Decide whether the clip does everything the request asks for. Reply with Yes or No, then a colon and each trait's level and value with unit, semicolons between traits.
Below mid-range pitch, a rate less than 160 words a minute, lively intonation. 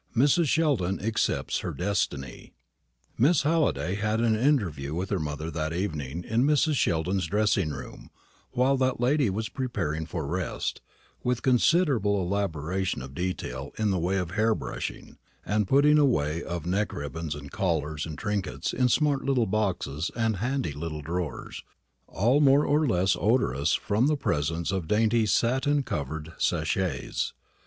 Yes: very low, 95 Hz; average, 150 wpm; wide, 7.5 semitones